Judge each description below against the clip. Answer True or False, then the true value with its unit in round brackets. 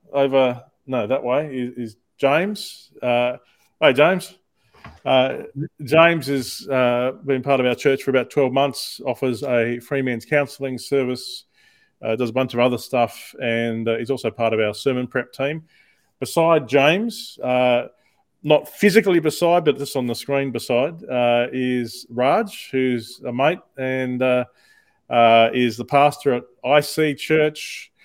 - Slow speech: False (160 wpm)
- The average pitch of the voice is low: True (130 Hz)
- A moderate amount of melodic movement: True (3.0 semitones)